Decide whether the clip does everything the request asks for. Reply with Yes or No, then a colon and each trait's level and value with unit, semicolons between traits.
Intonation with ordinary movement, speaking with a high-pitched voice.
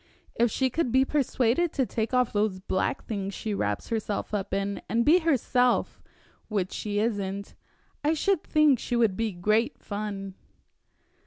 Yes: average, 4.4 semitones; high, 225 Hz